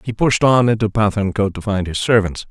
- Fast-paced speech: Yes, fast, 215 wpm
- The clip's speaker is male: Yes, male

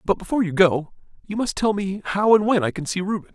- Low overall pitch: No, high, 190 Hz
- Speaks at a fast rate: Yes, fast, 270 wpm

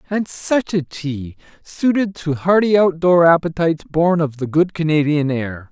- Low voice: No, medium, 165 Hz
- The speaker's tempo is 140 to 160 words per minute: Yes, average, 155 wpm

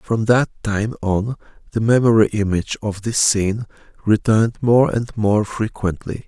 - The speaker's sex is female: No, male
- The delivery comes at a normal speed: Yes, average, 145 wpm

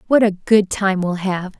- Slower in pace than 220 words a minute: No, fast, 225 wpm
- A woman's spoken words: Yes, female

